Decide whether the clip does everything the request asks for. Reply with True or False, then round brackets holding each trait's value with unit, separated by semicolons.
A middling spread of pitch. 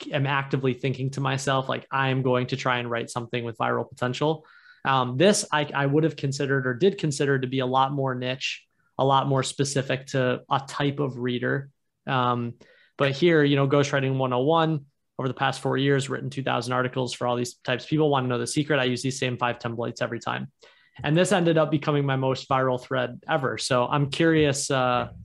False (2.2 semitones)